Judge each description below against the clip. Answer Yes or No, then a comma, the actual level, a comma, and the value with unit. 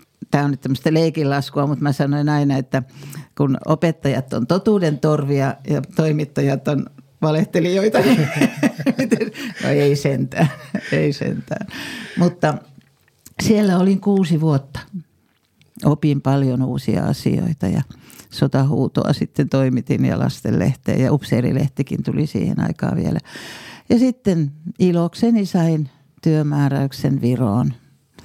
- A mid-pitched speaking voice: Yes, medium, 150 Hz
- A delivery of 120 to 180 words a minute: No, average, 110 wpm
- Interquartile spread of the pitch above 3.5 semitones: Yes, average, 4.2 semitones